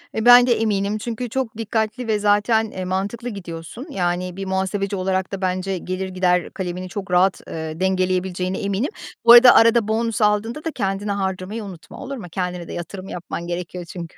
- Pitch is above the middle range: Yes, high, 195 Hz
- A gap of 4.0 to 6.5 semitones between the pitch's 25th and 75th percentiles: No, average, 3.2 semitones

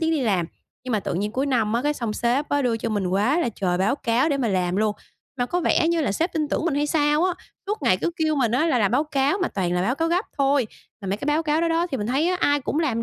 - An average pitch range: No, wide, 6.4 semitones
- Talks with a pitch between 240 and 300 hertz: Yes, very high, 270 Hz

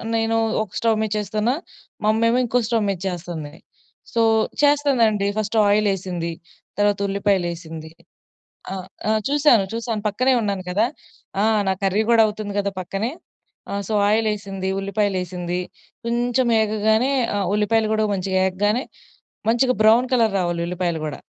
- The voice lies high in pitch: Yes, high, 210 Hz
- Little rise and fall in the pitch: No, average, 3.2 semitones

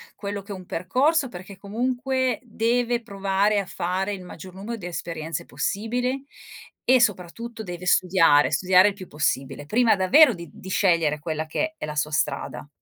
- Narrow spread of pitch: No, average, 5.2 semitones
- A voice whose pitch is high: Yes, high, 195 Hz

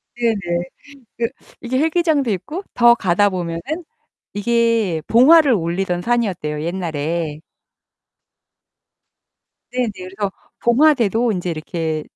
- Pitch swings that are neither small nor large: No, wide, 5.8 semitones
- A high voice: Yes, high, 205 Hz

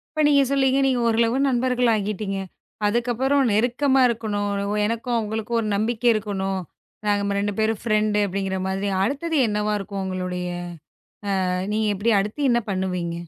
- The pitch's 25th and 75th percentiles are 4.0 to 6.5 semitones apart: No, average, 3.4 semitones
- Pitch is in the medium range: No, high, 215 Hz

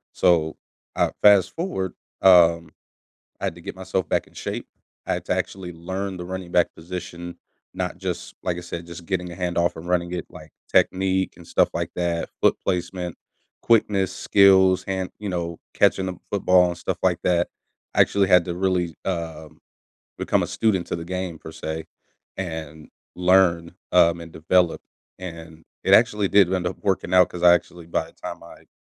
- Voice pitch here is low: Yes, very low, 90 Hz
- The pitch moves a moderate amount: No, narrow, 1.8 semitones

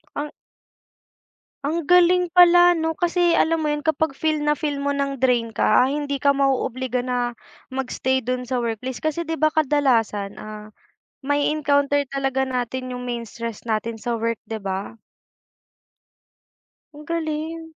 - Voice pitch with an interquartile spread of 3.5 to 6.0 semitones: Yes, average, 4.1 semitones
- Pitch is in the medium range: No, very high, 275 Hz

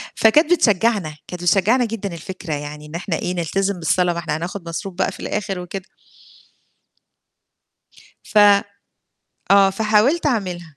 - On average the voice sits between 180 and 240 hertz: Yes, high, 190 Hz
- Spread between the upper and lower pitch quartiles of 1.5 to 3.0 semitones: No, average, 3.7 semitones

